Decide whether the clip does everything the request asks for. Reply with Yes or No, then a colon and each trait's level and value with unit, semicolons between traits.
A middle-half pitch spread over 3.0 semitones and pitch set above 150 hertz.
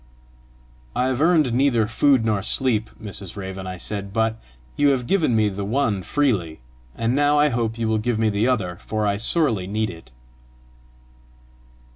No: average, 4.3 semitones; low, 110 Hz